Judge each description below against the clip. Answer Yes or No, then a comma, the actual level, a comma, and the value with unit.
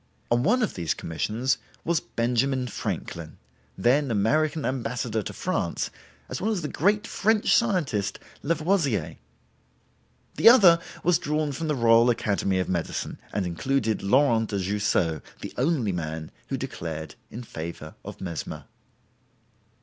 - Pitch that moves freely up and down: Yes, wide, 7.9 semitones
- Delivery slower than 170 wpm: Yes, slow, 135 wpm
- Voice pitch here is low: Yes, low, 120 Hz